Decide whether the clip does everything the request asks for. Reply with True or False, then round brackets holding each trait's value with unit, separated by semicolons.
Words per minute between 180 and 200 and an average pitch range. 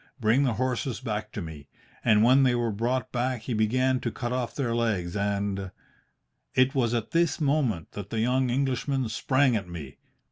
True (190 wpm; 3.6 semitones)